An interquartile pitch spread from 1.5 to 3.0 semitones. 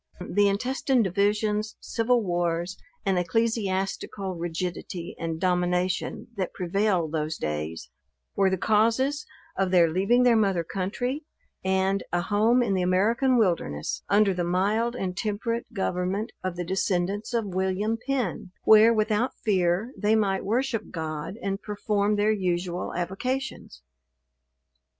No: average, 3.5 semitones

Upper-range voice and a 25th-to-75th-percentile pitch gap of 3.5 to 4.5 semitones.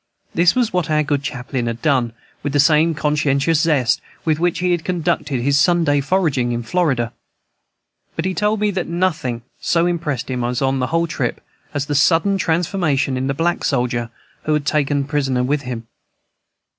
No: medium, 150 Hz; average, 4.2 semitones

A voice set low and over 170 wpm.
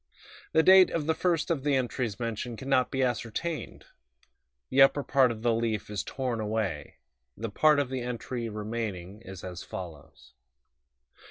No: low, 120 Hz; average, 165 wpm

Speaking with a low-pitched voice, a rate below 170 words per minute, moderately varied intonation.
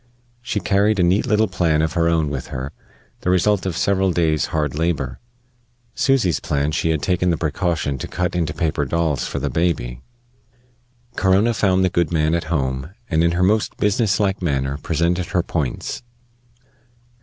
No: very low, 85 Hz; average, 175 wpm; average, 3.5 semitones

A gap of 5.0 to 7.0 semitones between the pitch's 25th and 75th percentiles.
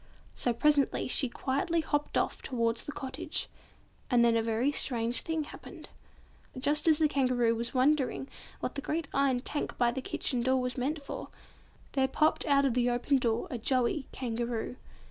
No: average, 3.2 semitones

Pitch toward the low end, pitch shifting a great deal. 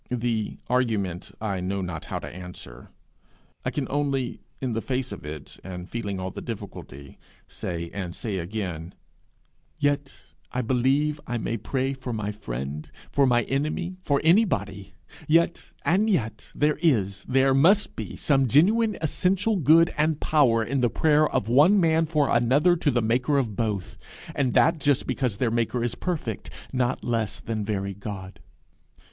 Yes: low, 125 Hz; wide, 6.4 semitones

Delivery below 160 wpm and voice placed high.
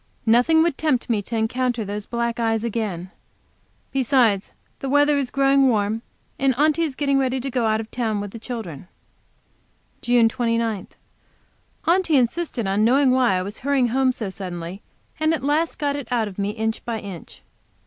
No: average, 180 wpm; high, 240 Hz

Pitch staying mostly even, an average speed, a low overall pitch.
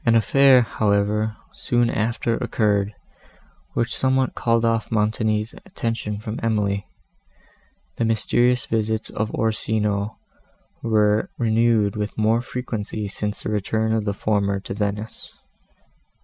No: narrow, 1.7 semitones; slow, 120 wpm; low, 110 Hz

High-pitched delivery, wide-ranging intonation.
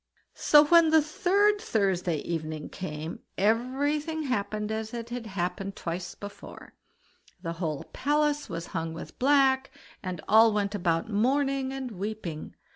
Yes: high, 220 Hz; wide, 7.7 semitones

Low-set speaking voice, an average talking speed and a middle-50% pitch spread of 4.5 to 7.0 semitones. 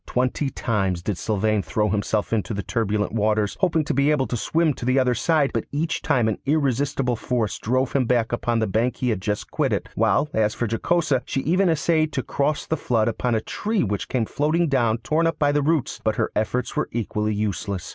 No: low, 120 Hz; fast, 215 wpm; average, 5.1 semitones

